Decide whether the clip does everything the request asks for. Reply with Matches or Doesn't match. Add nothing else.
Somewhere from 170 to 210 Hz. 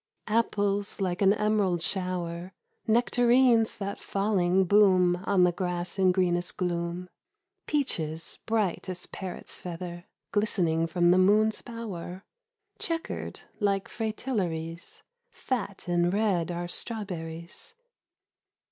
Matches